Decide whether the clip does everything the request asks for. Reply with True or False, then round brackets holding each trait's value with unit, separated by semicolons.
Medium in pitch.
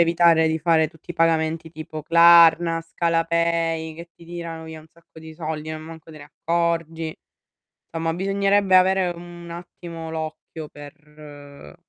True (165 Hz)